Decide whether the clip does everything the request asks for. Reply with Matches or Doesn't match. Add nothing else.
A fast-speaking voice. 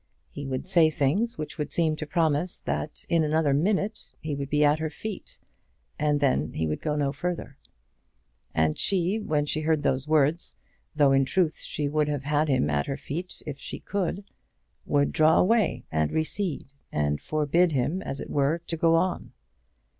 Doesn't match